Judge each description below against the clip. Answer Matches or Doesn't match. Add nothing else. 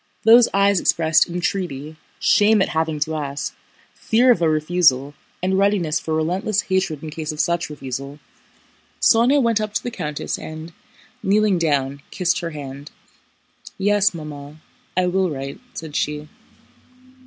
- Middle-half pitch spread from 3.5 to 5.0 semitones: Matches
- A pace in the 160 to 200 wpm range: Doesn't match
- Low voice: Doesn't match